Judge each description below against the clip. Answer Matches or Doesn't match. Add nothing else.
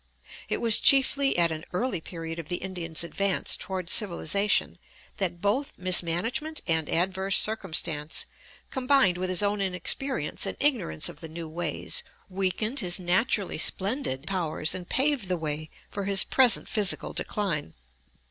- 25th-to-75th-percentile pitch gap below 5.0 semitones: Matches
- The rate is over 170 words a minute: Doesn't match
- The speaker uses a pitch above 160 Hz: Matches